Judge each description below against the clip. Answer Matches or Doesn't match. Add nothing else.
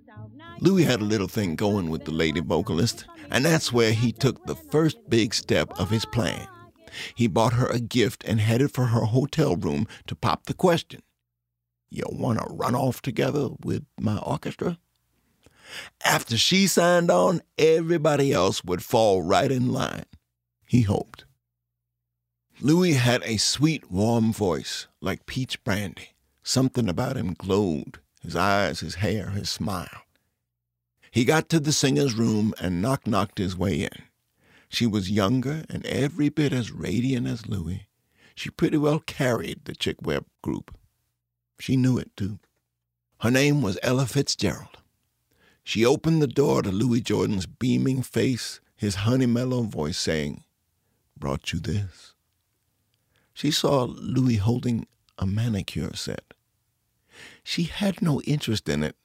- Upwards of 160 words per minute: Doesn't match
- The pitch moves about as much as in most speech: Doesn't match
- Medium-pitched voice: Doesn't match